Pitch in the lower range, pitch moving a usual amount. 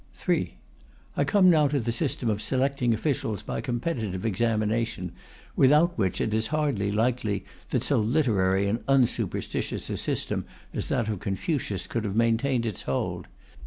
Yes: low, 115 Hz; average, 4.6 semitones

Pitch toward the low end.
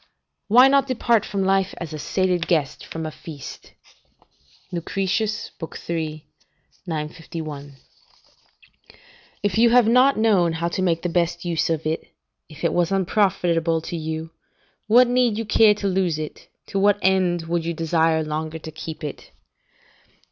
No: medium, 170 Hz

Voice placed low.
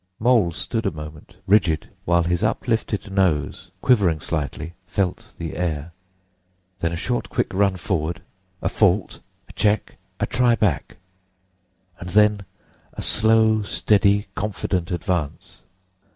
Yes: very low, 95 Hz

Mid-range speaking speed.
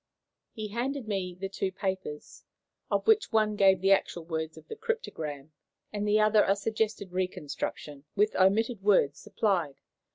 Yes: average, 160 wpm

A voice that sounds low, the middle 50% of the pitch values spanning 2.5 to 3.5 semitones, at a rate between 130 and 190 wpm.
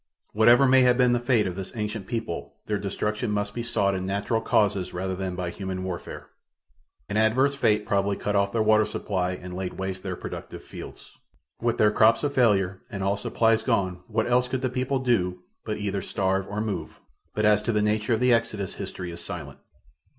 No: low, 105 Hz; average, 3.2 semitones; fast, 205 wpm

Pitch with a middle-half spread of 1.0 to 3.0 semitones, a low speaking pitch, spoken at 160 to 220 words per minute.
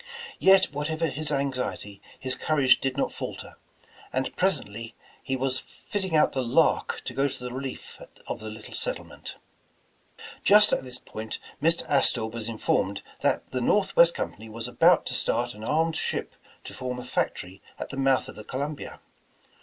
No: average, 4.5 semitones; low, 130 Hz; average, 170 wpm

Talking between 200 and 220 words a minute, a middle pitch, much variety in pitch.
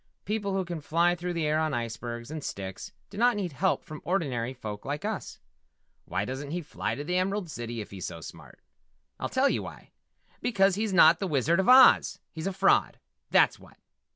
Yes: fast, 205 wpm; medium, 165 Hz; wide, 6.6 semitones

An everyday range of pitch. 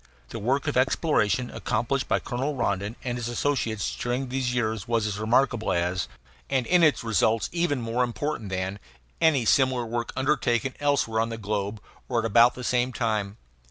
Yes: average, 3.2 semitones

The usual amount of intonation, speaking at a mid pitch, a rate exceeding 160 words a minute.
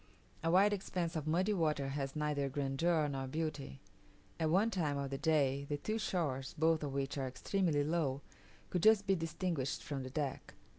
Yes: average, 3.9 semitones; medium, 150 Hz; average, 185 wpm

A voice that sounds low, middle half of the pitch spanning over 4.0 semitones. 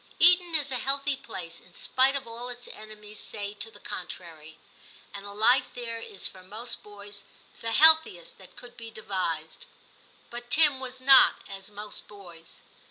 No: high, 225 Hz; average, 4.4 semitones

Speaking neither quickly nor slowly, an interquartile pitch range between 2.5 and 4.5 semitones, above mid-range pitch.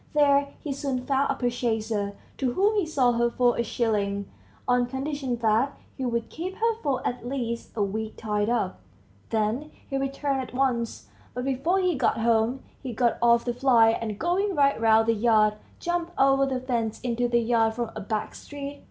Yes: average, 190 wpm; average, 3.5 semitones; high, 245 Hz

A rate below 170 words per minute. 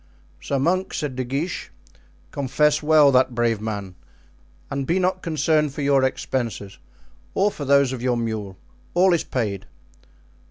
Yes: average, 150 wpm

